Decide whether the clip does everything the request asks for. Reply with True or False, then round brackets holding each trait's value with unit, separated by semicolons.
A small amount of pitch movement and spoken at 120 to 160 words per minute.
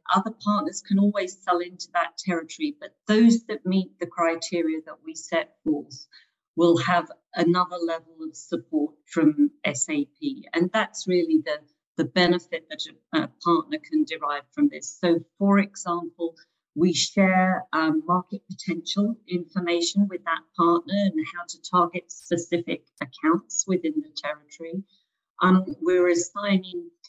False (4.1 semitones; 140 wpm)